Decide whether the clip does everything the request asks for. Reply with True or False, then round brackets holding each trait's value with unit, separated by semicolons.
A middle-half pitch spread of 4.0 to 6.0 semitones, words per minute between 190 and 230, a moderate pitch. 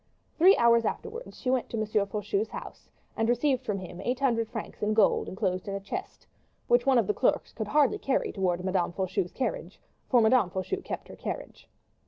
False (5.0 semitones; 200 wpm; 230 Hz)